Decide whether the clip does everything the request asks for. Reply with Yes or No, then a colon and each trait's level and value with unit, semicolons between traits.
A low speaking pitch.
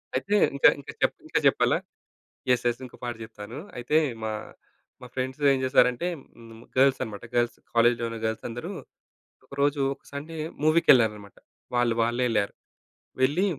Yes: low, 120 Hz